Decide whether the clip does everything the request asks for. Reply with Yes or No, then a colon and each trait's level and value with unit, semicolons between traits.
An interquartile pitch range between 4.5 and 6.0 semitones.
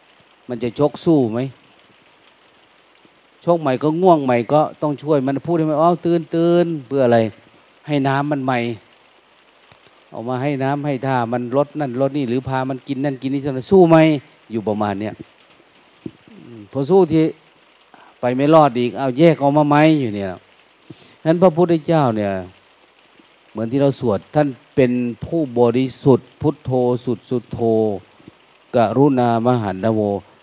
No: average, 3.9 semitones